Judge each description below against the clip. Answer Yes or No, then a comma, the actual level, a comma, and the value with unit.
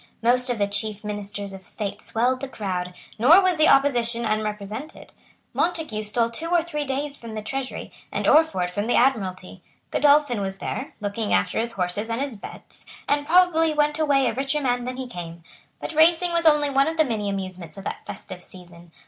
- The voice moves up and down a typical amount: No, wide, 6.3 semitones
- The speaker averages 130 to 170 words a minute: No, average, 195 wpm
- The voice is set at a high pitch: Yes, high, 235 Hz